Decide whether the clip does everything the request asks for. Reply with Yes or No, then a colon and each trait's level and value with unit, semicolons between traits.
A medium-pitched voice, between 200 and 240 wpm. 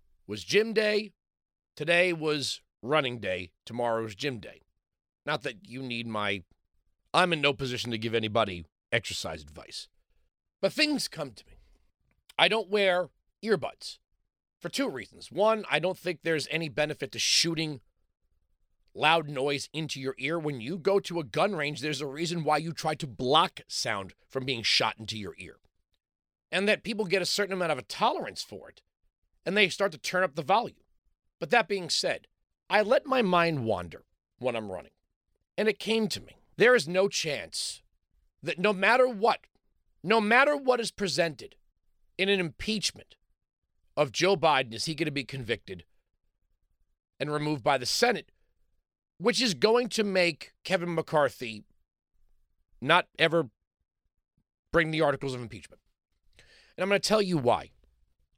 No: medium, 150 Hz; average, 165 wpm